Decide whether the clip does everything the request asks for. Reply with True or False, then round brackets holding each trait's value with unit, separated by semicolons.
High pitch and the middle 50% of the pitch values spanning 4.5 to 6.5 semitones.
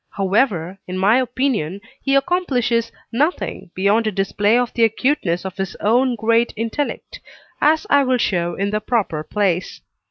True (220 Hz; 4.8 semitones)